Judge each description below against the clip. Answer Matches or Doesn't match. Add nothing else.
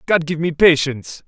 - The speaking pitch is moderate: Matches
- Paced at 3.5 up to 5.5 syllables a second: Matches